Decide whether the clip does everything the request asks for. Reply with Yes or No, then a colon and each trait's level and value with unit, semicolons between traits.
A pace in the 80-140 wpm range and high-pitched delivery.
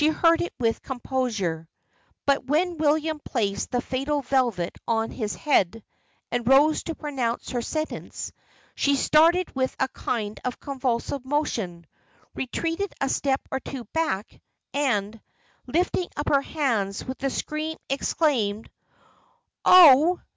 Yes: slow, 135 wpm; very high, 270 Hz